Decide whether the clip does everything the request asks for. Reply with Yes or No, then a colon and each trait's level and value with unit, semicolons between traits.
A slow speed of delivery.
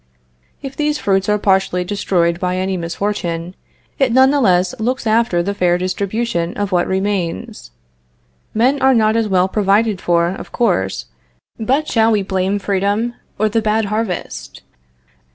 No: average, 155 wpm